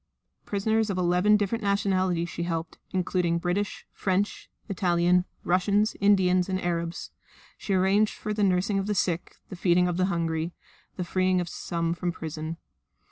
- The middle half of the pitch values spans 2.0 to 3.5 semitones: Yes, narrow, 2.4 semitones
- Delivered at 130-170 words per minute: Yes, average, 155 wpm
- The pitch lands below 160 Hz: No, medium, 180 Hz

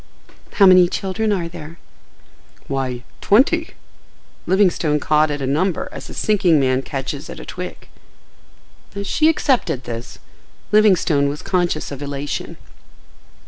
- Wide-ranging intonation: Yes, wide, 5.7 semitones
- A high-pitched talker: No, medium, 165 Hz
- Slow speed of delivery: Yes, slow, 125 wpm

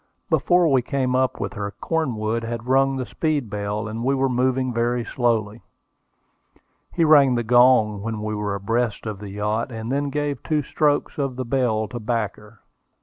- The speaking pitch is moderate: No, low, 120 Hz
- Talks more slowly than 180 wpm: No, average, 185 wpm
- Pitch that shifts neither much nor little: Yes, average, 3.8 semitones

